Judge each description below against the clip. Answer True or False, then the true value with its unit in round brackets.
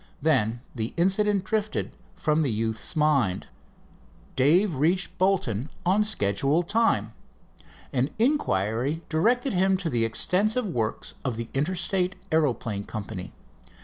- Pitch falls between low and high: True (155 Hz)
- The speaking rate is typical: False (115 wpm)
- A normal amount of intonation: False (8.7 semitones)